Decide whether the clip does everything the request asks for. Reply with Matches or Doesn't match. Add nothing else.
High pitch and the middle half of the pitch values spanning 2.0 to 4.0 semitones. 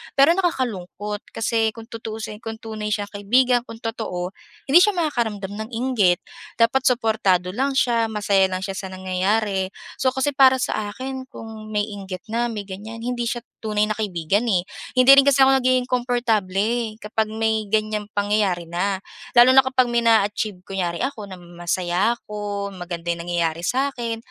Matches